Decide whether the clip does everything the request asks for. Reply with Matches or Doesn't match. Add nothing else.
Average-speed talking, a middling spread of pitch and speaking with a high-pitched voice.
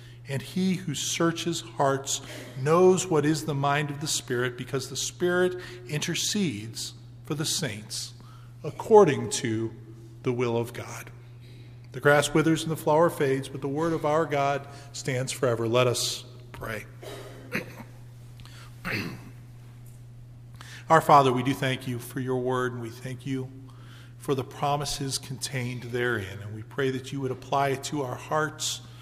Doesn't match